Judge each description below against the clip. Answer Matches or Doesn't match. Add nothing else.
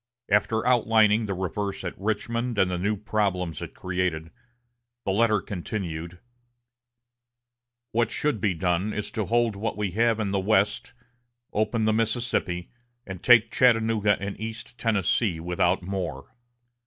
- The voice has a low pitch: Matches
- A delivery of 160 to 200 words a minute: Doesn't match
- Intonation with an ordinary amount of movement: Matches